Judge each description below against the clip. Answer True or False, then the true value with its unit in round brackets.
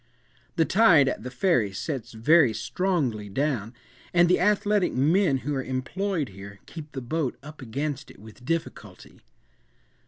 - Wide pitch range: True (6.1 semitones)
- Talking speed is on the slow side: False (150 wpm)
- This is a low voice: False (145 Hz)